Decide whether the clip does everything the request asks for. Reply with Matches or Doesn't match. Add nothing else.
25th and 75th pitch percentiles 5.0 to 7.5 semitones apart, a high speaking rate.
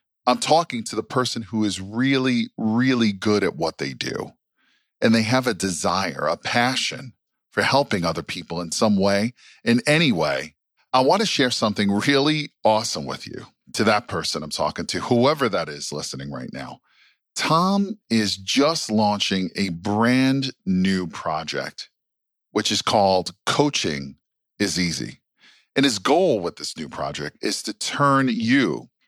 Doesn't match